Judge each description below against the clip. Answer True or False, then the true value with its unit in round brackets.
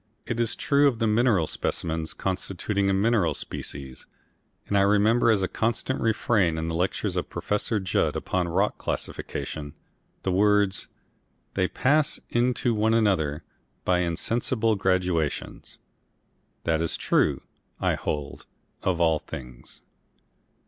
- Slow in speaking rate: True (130 wpm)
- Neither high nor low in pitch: False (95 Hz)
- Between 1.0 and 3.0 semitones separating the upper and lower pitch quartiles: False (5.2 semitones)